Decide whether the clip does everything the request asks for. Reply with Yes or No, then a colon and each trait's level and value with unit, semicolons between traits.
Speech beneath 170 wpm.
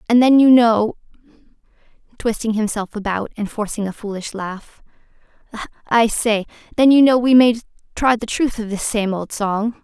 Yes: average, 155 wpm